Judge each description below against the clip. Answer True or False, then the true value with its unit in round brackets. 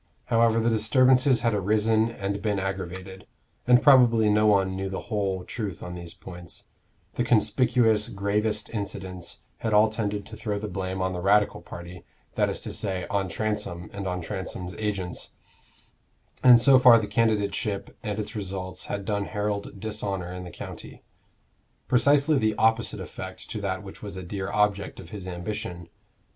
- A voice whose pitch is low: True (105 Hz)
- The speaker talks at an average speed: True (165 wpm)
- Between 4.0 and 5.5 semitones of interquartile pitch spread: False (2.7 semitones)